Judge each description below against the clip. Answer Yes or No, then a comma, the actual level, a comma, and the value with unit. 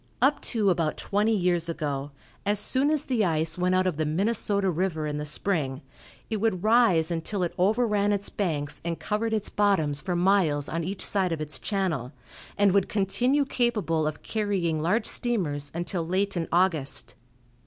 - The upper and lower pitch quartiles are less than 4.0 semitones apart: No, average, 4.5 semitones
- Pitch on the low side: No, medium, 185 Hz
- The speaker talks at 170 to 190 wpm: Yes, average, 175 wpm